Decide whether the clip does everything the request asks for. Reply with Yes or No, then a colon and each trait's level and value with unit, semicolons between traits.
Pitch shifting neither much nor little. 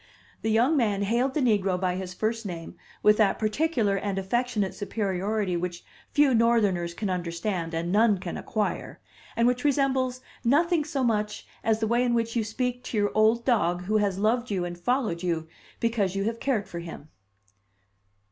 Yes: average, 4.2 semitones